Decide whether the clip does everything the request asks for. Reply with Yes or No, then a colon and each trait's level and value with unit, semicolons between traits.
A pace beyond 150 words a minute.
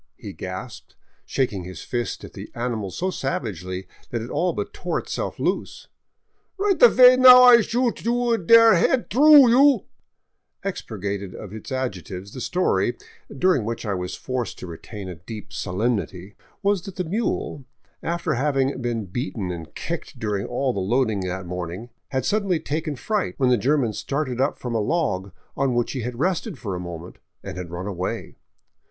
Yes: average, 180 wpm